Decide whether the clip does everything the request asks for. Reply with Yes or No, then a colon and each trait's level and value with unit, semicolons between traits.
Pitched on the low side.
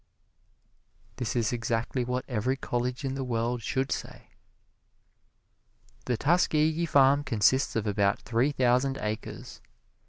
Yes: low, 125 Hz